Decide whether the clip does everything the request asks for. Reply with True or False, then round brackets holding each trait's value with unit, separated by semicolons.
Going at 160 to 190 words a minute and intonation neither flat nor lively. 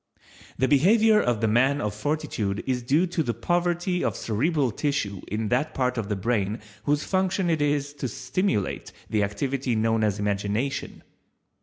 False (165 wpm; 5.9 semitones)